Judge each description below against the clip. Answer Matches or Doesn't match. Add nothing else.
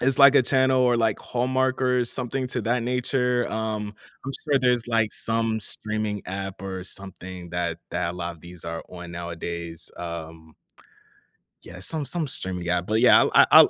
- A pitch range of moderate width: Doesn't match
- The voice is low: Matches